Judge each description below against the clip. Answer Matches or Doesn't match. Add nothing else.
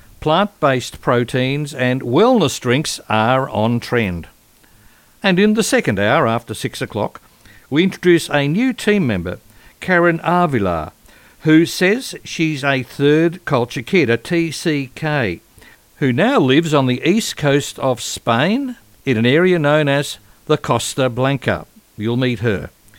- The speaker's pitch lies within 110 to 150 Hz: Matches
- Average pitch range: Doesn't match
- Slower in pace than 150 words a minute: Matches